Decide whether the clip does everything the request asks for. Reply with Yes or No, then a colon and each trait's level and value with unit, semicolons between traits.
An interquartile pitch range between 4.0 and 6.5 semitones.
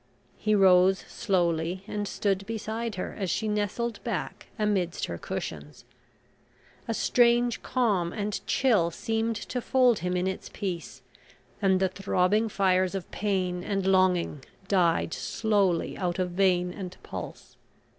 No: average, 3.0 semitones